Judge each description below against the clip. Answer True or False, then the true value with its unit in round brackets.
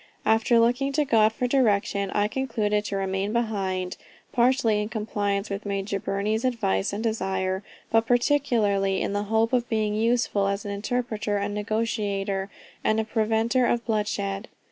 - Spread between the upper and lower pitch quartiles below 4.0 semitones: True (2.6 semitones)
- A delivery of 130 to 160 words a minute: True (155 wpm)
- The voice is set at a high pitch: True (215 Hz)